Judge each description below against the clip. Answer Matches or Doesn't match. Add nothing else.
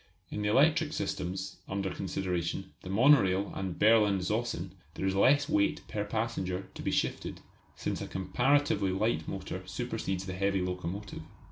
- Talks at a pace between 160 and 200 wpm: Doesn't match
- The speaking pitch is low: Matches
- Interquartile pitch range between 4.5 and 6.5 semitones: Doesn't match